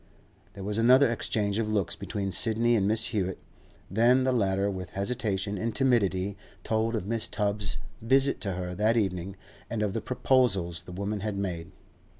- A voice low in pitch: Yes, low, 105 Hz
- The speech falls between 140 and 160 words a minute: No, average, 170 wpm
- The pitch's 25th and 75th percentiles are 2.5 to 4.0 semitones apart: Yes, average, 2.9 semitones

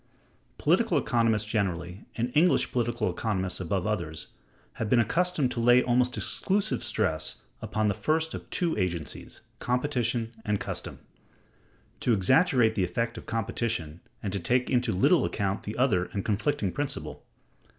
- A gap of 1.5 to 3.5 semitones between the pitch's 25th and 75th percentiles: No, average, 4.5 semitones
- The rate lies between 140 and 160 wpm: Yes, average, 145 wpm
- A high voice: No, low, 110 Hz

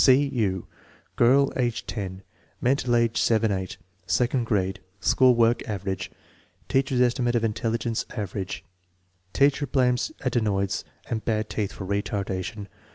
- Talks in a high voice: No, low, 115 Hz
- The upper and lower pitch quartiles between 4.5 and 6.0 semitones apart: No, average, 3.6 semitones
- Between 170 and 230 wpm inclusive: No, slow, 135 wpm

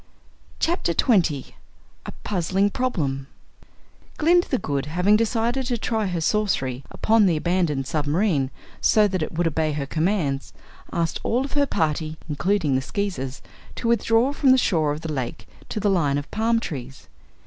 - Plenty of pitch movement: Yes, wide, 7.0 semitones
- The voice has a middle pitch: Yes, medium, 175 Hz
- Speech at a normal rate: Yes, average, 160 wpm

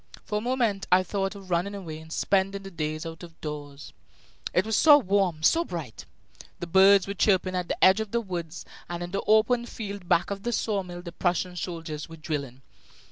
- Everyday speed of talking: No, fast, 210 wpm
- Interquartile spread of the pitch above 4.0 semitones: No, average, 3.3 semitones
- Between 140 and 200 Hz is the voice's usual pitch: Yes, medium, 185 Hz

